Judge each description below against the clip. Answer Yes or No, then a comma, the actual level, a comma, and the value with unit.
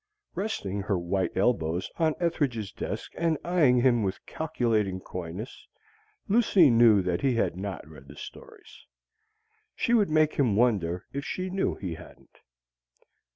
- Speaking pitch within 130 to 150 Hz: No, low, 115 Hz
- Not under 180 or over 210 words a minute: No, average, 145 wpm